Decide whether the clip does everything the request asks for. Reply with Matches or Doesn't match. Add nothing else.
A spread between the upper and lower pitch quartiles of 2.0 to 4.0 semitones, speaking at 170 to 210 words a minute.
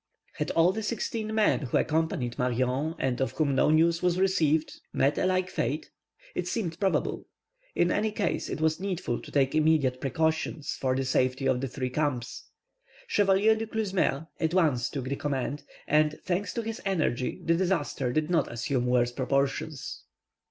Doesn't match